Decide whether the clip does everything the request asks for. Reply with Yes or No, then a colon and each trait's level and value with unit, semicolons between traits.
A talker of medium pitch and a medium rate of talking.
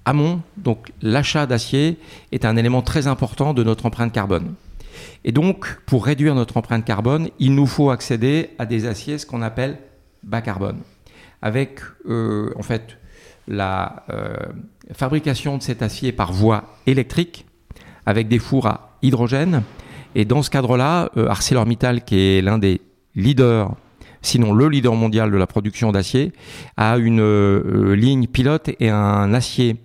No: low, 120 Hz; average, 155 wpm